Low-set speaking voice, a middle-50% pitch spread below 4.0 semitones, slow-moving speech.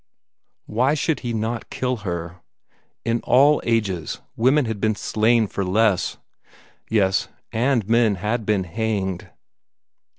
Yes: low, 110 Hz; average, 3.3 semitones; slow, 125 wpm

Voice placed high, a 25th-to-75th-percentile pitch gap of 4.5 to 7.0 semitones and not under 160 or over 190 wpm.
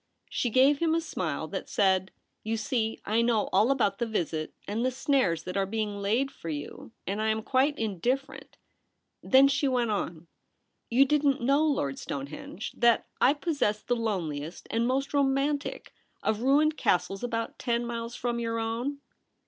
Yes: high, 235 Hz; average, 4.9 semitones; average, 175 wpm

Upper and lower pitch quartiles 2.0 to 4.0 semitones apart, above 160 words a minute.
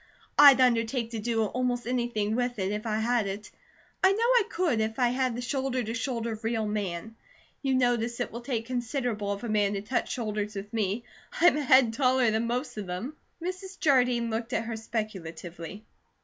Yes: average, 2.9 semitones; average, 195 wpm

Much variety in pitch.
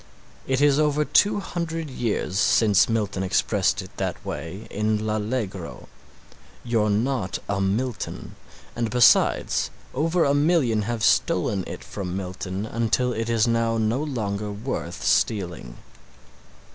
No: average, 4.4 semitones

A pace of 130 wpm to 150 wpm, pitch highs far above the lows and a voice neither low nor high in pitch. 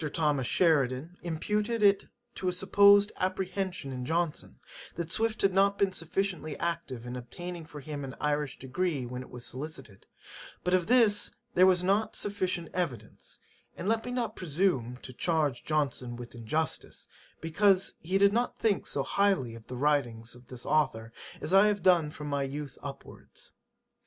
No: average, 165 wpm; wide, 6.4 semitones; medium, 165 Hz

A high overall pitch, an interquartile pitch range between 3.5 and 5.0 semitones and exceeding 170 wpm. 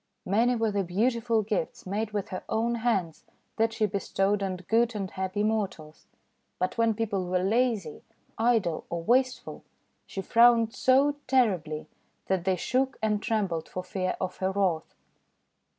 No: high, 210 Hz; average, 3.8 semitones; average, 150 wpm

